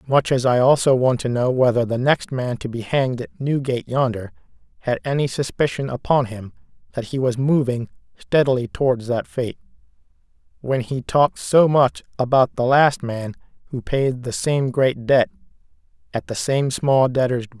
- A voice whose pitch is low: Yes, low, 130 Hz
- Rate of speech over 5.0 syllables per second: No, 4.9 syllables/s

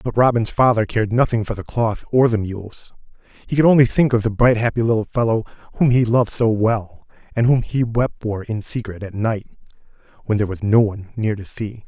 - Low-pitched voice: Yes, low, 110 Hz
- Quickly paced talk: Yes, fast, 215 wpm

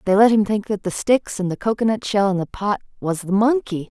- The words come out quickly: Yes, fast, 255 wpm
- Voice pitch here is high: Yes, high, 205 Hz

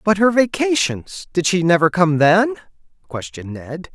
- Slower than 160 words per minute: Yes, slow, 135 wpm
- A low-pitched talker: No, medium, 180 Hz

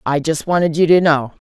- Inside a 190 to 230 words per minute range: No, fast, 245 wpm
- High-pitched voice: No, medium, 160 Hz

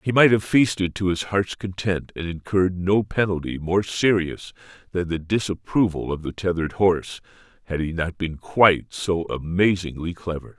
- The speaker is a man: Yes, male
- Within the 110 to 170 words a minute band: Yes, average, 165 wpm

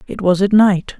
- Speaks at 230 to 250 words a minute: Yes, fast, 240 wpm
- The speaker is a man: No, female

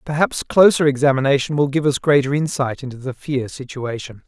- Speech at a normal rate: Yes, average, 170 wpm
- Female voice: No, male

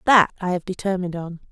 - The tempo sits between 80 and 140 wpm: No, average, 200 wpm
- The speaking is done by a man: No, female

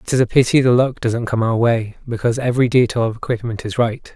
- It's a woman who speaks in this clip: No, male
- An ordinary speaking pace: No, fast, 245 wpm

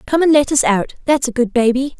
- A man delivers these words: No, female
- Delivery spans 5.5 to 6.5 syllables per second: Yes, 5.8 syllables/s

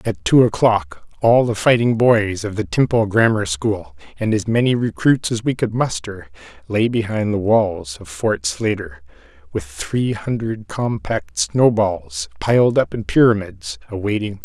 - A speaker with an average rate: Yes, average, 175 wpm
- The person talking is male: Yes, male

